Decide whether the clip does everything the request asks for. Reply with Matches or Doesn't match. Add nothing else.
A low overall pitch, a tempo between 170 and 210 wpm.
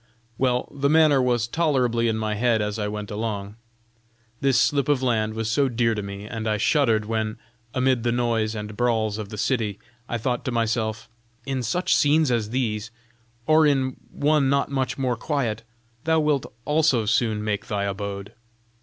Matches